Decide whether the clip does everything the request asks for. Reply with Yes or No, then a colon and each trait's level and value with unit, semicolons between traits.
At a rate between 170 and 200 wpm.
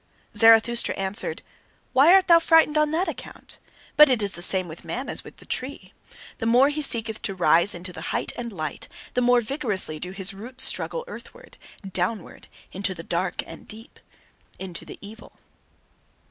Yes: average, 175 wpm